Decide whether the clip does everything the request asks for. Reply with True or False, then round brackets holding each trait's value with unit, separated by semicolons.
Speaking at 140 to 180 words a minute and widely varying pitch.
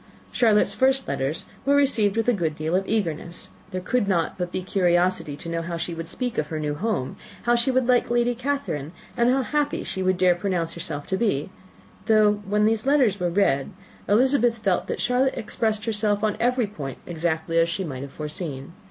False (205 wpm; 6.0 semitones)